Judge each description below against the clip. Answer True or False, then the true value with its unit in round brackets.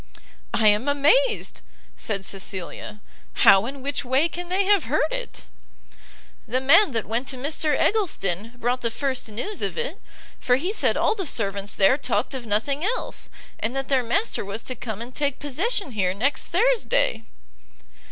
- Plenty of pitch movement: True (7.3 semitones)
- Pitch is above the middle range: True (265 Hz)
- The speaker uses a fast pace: False (170 wpm)